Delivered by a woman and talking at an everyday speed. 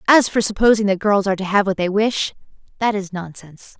No: female; fast, 220 wpm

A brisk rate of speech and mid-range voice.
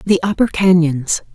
No: slow, 135 wpm; medium, 175 Hz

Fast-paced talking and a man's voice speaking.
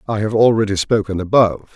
No: average, 170 wpm; male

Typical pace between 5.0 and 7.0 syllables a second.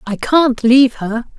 No: 4.2 syllables/s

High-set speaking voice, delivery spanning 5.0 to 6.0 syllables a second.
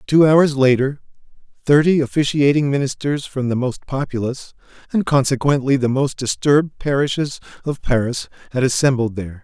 No: low, 135 Hz; 5.3 syllables/s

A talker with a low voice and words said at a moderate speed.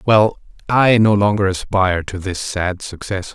Yes: low, 100 Hz; average, 160 wpm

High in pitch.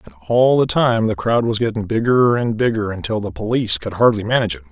No: low, 110 Hz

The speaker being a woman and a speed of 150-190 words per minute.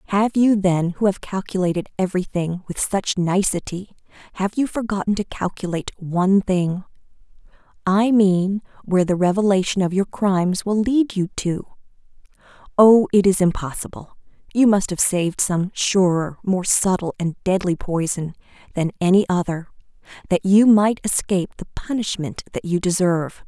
No: female; average, 140 wpm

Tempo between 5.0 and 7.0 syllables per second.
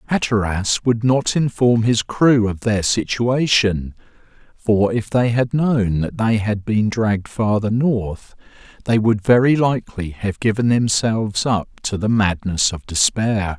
No: 4.0 syllables/s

